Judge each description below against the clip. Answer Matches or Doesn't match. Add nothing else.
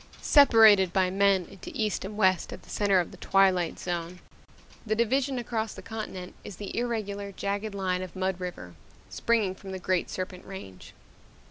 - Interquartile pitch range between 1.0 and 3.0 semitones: Matches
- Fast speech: Doesn't match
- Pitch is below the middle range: Doesn't match